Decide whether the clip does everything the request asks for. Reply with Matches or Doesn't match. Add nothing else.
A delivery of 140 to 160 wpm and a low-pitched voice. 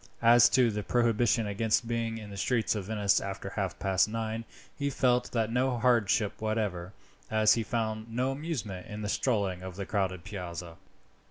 Doesn't match